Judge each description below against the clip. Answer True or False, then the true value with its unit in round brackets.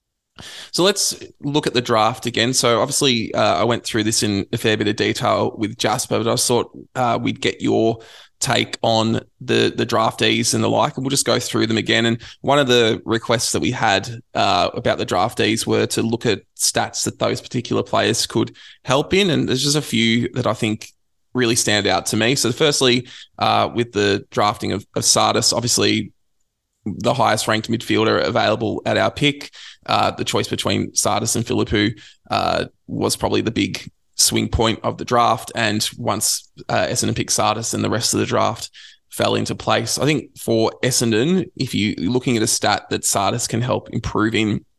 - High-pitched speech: False (115 Hz)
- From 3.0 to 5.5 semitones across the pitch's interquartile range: False (2.5 semitones)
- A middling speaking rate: True (195 wpm)